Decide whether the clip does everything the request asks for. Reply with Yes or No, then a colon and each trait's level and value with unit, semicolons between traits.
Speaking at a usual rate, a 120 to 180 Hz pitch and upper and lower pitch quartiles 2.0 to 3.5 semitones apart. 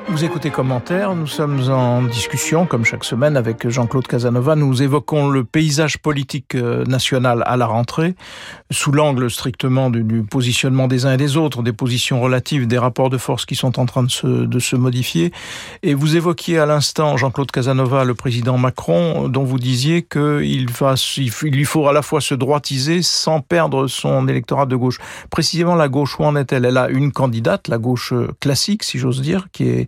Yes: average, 190 wpm; low, 135 Hz; average, 3.1 semitones